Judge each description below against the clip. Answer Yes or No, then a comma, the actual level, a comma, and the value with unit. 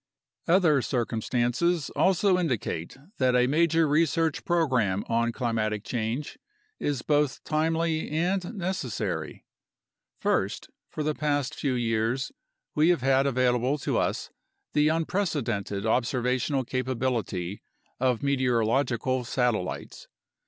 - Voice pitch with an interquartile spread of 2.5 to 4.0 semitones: No, average, 4.8 semitones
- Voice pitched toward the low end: Yes, low, 130 Hz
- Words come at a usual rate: No, slow, 105 wpm